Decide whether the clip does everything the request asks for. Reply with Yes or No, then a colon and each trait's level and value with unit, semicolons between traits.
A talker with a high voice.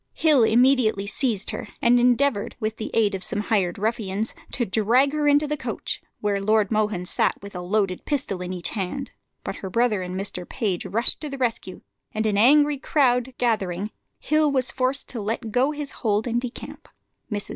Yes: high, 225 Hz